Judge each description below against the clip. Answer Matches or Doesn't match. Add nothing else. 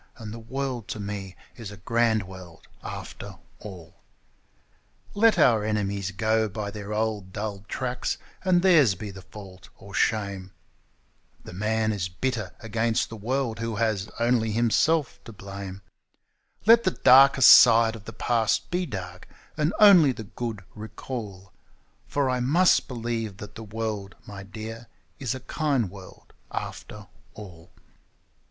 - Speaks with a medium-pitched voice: Doesn't match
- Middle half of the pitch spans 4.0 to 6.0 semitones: Doesn't match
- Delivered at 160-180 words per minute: Doesn't match